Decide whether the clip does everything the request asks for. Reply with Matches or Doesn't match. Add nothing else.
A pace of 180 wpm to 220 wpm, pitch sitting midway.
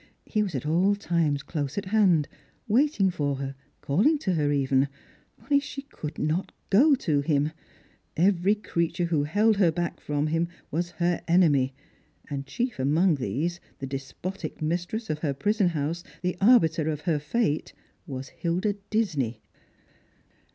Doesn't match